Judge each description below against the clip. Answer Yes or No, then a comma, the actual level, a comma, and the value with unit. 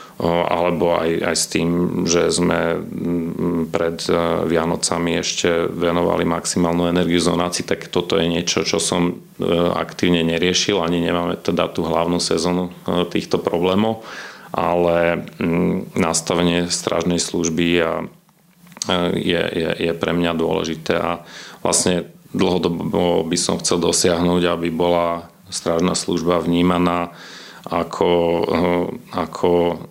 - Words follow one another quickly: No, slow, 110 wpm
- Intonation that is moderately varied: No, narrow, 0.7 semitones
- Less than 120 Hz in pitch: Yes, very low, 85 Hz